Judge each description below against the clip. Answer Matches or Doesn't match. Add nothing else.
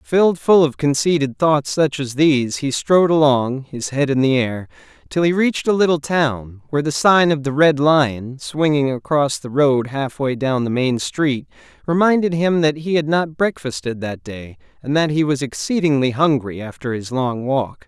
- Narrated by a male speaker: Matches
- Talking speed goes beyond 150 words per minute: Matches